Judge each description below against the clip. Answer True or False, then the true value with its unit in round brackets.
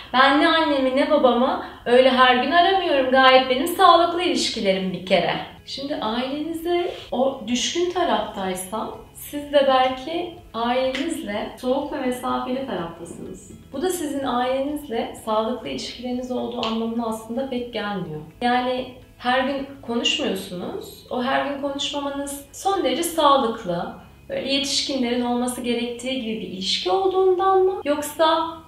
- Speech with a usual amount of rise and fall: True (3.6 semitones)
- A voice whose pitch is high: True (260 Hz)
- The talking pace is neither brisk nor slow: True (125 wpm)